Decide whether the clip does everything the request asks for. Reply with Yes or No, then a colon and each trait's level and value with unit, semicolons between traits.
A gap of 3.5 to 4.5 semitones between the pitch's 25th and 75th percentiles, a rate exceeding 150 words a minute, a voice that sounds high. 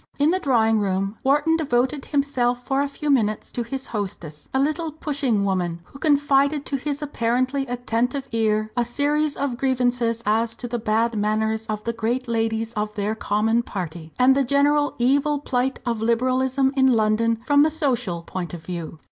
Yes: average, 4.1 semitones; average, 180 wpm; high, 245 Hz